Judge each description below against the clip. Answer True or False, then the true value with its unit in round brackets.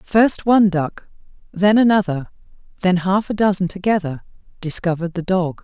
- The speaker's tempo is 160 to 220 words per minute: False (140 wpm)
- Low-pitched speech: False (185 Hz)